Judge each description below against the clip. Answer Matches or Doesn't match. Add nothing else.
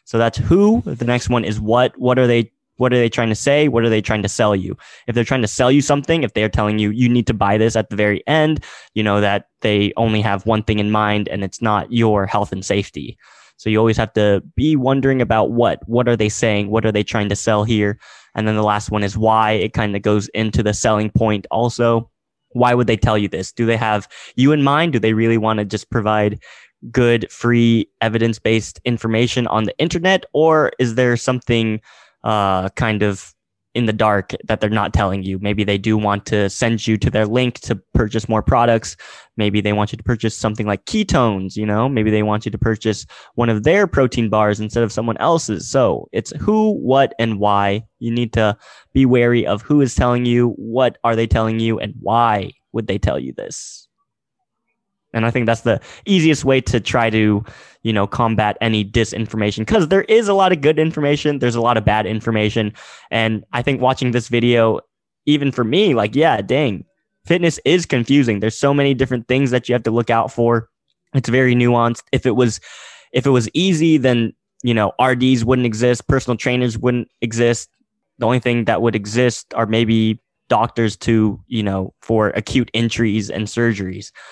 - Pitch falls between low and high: Doesn't match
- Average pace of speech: Doesn't match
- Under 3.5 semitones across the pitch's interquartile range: Matches